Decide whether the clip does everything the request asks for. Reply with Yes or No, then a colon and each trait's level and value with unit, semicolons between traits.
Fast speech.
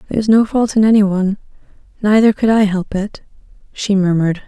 No: average, 190 wpm